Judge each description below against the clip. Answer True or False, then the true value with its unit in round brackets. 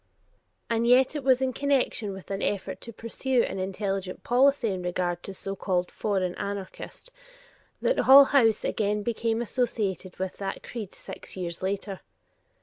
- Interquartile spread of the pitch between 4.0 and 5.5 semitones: True (4.3 semitones)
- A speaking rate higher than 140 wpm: True (160 wpm)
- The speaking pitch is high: True (205 Hz)